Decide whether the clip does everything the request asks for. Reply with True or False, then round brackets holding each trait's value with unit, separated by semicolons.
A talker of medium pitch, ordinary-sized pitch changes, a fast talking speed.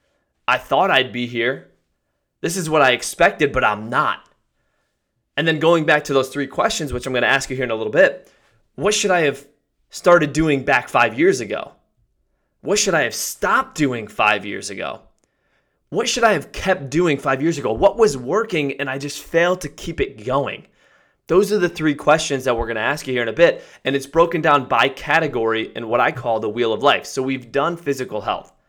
True (145 Hz; 4.5 semitones; 220 wpm)